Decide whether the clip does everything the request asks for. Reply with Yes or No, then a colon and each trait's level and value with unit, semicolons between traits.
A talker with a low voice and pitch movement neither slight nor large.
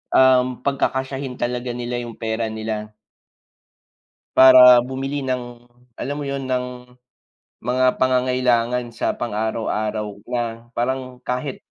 No: low, 125 Hz; narrow, 1.8 semitones